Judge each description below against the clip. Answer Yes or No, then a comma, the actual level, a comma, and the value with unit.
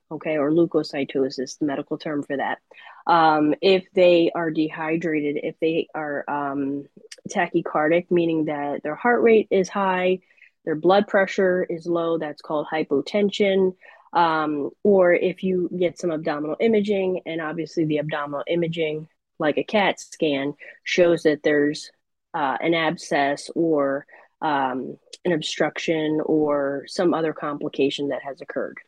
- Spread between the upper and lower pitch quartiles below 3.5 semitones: Yes, average, 3.0 semitones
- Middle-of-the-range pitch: Yes, medium, 160 Hz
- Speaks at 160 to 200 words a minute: No, average, 140 wpm